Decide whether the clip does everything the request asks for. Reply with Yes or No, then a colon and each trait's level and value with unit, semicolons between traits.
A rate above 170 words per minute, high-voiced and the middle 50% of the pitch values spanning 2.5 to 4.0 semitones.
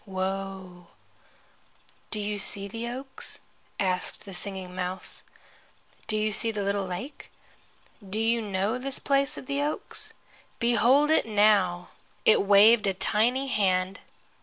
No: slow, 135 wpm; high, 205 Hz; average, 3.6 semitones